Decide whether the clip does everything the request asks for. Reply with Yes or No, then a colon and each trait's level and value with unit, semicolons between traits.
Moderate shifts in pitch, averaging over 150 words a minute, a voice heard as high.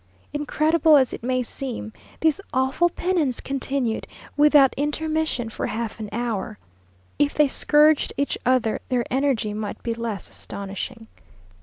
No: average, 4.4 semitones; slow, 135 wpm; very high, 260 Hz